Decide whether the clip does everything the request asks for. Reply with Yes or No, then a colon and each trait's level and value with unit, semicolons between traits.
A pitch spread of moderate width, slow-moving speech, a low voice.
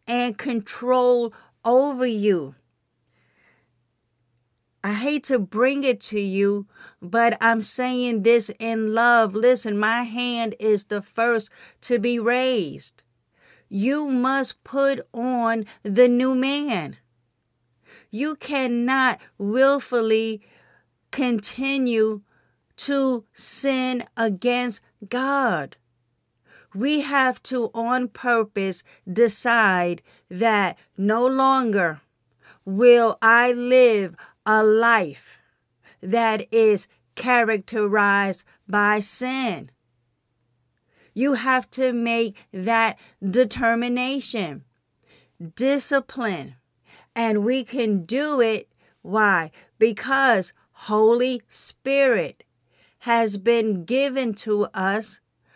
No: average, 3.8 semitones; slow, 85 wpm; high, 230 Hz